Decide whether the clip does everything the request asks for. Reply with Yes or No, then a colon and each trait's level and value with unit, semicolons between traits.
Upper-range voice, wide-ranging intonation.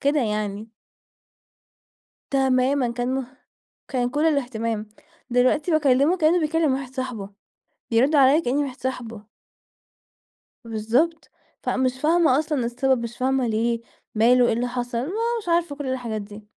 No: very high, 255 Hz; average, 3.4 semitones